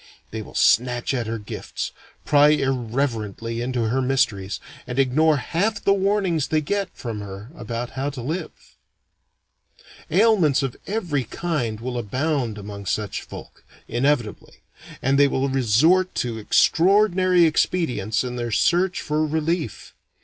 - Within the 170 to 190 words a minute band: No, slow, 135 wpm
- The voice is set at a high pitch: No, low, 135 Hz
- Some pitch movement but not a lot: No, wide, 5.8 semitones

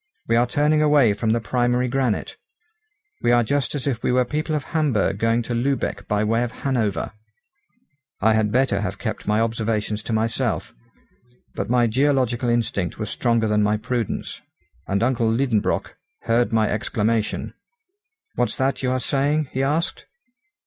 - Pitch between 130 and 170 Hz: No, low, 120 Hz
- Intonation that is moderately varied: Yes, average, 3.2 semitones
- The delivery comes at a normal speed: Yes, average, 165 wpm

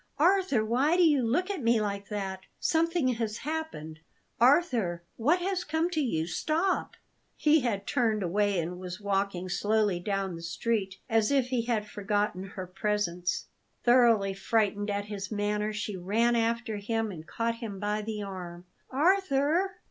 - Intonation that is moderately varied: Yes, average, 4.9 semitones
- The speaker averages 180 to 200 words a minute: No, average, 160 wpm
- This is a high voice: Yes, high, 215 Hz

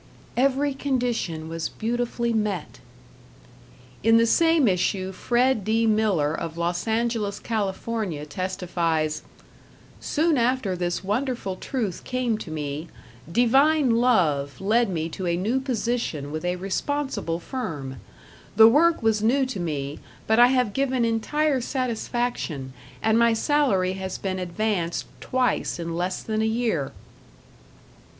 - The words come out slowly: Yes, slow, 130 wpm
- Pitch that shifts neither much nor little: No, wide, 5.9 semitones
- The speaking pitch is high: Yes, high, 220 Hz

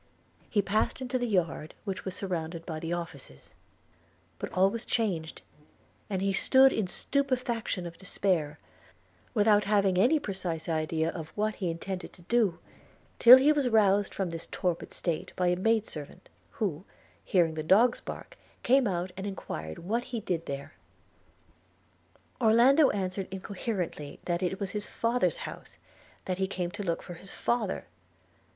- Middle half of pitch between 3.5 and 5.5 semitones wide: Yes, average, 4.4 semitones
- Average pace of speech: Yes, average, 160 wpm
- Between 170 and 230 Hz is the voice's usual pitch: Yes, high, 190 Hz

